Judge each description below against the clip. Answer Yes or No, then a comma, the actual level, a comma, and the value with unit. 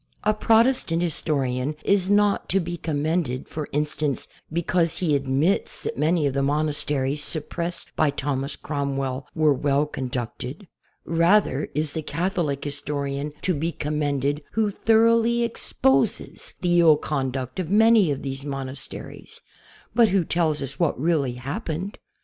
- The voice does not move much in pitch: No, average, 4.0 semitones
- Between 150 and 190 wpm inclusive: No, average, 140 wpm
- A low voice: No, medium, 150 Hz